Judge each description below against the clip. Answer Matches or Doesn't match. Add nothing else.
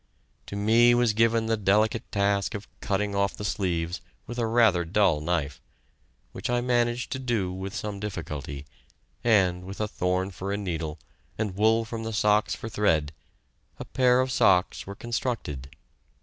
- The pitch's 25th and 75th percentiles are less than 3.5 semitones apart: Doesn't match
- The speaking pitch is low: Matches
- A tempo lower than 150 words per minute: Doesn't match